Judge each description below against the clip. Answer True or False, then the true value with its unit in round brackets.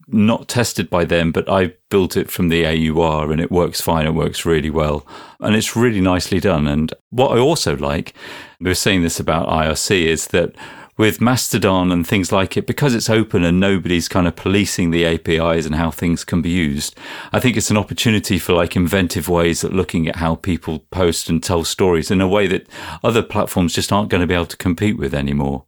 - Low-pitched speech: True (85 Hz)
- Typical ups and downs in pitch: True (3.5 semitones)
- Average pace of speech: False (210 wpm)